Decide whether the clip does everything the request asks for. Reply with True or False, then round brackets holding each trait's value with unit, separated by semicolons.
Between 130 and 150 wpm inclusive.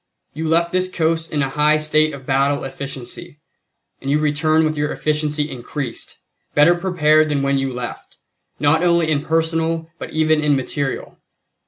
False (165 wpm)